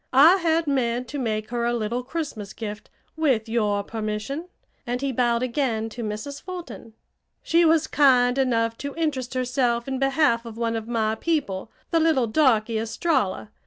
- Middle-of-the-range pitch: No, high, 245 Hz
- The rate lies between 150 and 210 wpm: Yes, average, 165 wpm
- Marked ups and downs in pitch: No, average, 4.1 semitones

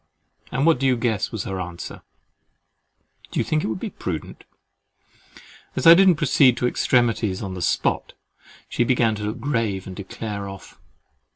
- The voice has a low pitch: Yes, low, 115 Hz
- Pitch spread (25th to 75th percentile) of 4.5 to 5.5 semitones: Yes, average, 4.9 semitones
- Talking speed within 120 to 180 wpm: Yes, average, 165 wpm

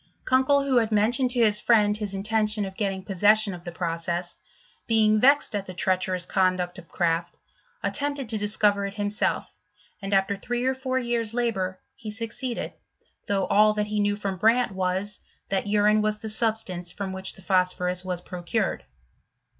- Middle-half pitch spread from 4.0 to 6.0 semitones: No, average, 3.0 semitones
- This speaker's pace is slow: No, average, 170 wpm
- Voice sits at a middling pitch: No, high, 205 Hz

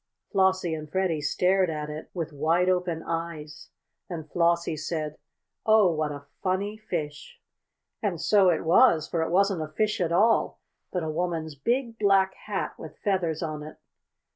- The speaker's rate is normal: Yes, average, 165 wpm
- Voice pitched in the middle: Yes, medium, 170 Hz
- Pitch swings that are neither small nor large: Yes, average, 3.5 semitones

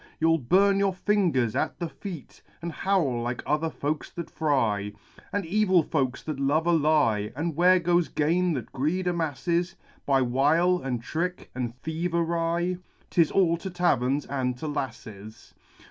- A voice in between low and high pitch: Yes, medium, 160 Hz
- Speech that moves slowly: No, average, 155 wpm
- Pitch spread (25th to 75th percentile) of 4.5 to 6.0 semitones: Yes, average, 4.9 semitones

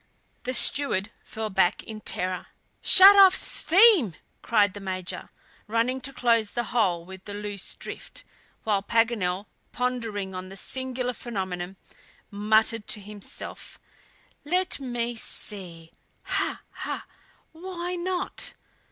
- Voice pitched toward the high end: Yes, high, 220 Hz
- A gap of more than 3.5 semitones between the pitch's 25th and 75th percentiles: Yes, average, 4.8 semitones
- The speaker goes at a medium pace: No, slow, 120 wpm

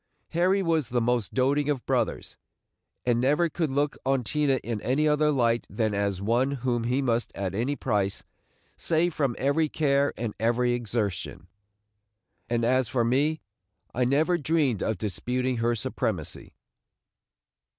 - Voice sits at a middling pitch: No, low, 125 Hz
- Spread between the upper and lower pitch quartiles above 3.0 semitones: Yes, average, 3.9 semitones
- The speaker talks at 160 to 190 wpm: No, average, 150 wpm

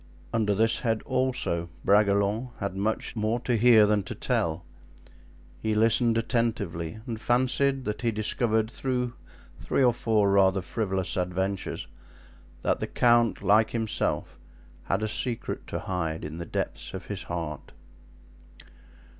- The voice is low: Yes, low, 110 Hz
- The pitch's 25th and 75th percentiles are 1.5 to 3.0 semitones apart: No, average, 3.5 semitones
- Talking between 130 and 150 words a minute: Yes, average, 140 wpm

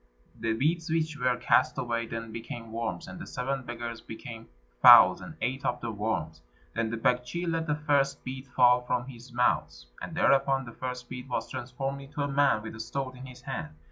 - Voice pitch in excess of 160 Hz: No, low, 125 Hz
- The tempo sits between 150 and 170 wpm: No, fast, 205 wpm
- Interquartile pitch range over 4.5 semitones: No, average, 3.0 semitones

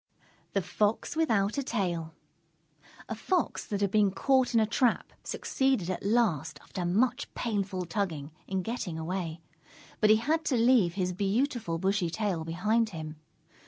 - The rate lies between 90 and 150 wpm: No, average, 160 wpm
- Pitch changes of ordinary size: Yes, average, 5.0 semitones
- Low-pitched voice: No, high, 200 Hz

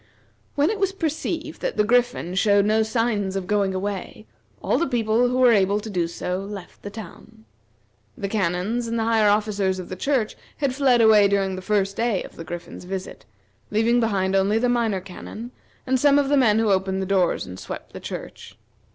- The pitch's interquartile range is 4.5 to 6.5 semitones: No, average, 3.8 semitones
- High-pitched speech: Yes, high, 210 Hz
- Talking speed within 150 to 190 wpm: No, fast, 205 wpm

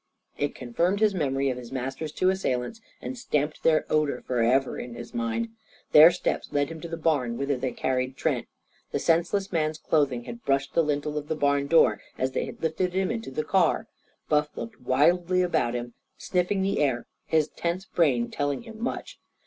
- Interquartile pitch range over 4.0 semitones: Yes, average, 5.2 semitones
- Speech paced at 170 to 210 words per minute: Yes, average, 195 wpm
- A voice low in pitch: No, medium, 150 Hz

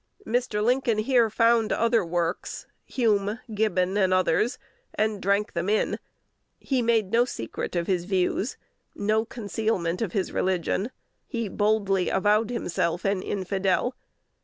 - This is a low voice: No, high, 205 Hz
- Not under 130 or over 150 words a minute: Yes, slow, 135 wpm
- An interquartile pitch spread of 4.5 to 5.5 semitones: No, average, 3.5 semitones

